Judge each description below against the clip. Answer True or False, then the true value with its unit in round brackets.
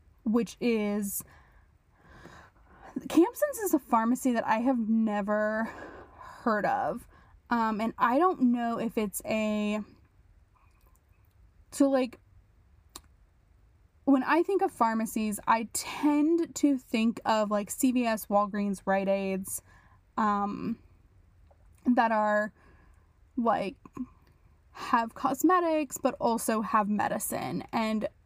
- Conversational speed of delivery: False (100 wpm)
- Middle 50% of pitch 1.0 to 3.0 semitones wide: False (5.1 semitones)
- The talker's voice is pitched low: False (220 Hz)